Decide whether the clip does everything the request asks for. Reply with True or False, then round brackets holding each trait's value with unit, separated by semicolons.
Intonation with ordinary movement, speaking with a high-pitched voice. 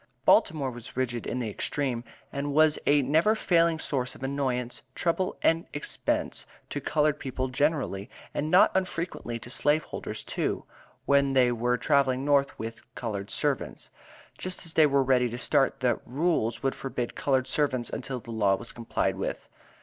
False (3.5 semitones; 135 Hz)